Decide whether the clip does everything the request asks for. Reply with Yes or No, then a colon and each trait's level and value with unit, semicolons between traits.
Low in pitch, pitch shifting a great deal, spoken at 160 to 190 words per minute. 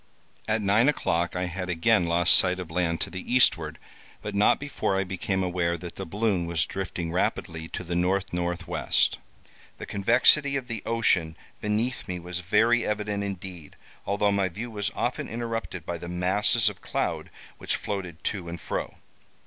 No: very low, 95 Hz; average, 3.3 semitones; average, 175 wpm